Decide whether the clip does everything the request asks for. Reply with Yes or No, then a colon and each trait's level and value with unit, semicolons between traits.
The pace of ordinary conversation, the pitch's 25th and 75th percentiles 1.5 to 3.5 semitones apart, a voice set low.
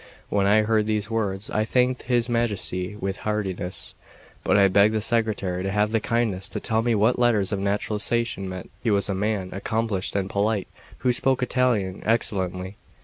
Yes: average, 180 wpm; average, 2.7 semitones; low, 105 Hz